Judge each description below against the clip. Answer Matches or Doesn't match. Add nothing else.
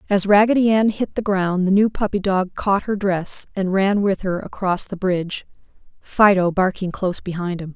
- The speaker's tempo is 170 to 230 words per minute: Matches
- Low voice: Doesn't match